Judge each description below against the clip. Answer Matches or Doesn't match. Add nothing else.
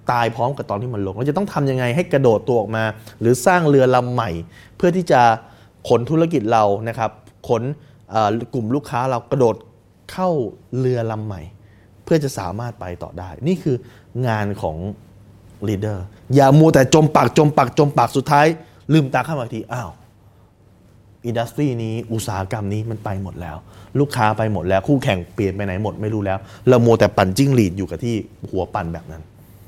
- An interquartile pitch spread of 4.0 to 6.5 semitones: Matches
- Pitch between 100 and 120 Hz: Matches